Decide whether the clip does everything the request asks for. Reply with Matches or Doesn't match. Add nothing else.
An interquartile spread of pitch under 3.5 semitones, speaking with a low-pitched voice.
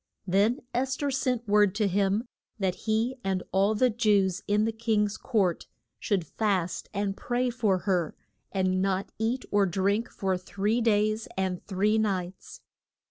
Doesn't match